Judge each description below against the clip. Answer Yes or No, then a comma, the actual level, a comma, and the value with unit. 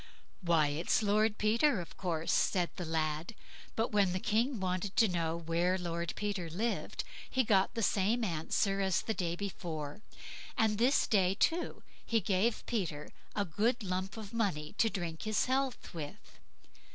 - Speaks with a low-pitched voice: No, high, 195 Hz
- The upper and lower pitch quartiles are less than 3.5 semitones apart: No, average, 4.4 semitones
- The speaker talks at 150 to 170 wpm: Yes, average, 165 wpm